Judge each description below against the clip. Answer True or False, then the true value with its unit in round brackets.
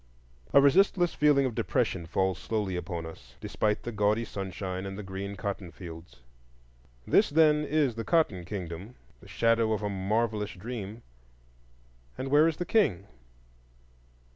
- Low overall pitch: True (105 Hz)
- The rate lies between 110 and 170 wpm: True (140 wpm)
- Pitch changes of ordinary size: False (6.1 semitones)